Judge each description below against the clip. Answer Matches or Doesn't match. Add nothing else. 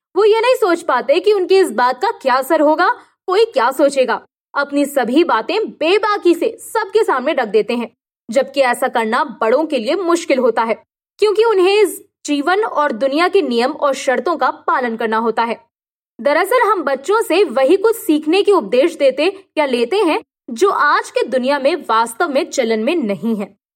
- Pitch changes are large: Matches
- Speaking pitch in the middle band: Doesn't match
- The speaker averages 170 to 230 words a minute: Matches